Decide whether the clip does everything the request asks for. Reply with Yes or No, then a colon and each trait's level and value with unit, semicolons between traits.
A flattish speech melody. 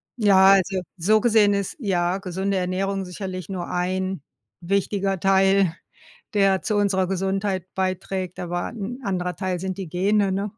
Yes: narrow, 1.3 semitones